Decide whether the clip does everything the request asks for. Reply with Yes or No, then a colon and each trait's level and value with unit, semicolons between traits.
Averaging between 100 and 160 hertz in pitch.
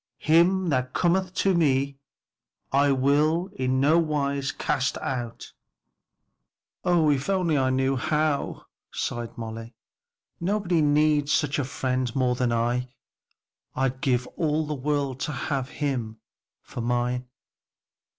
Yes: medium, 140 Hz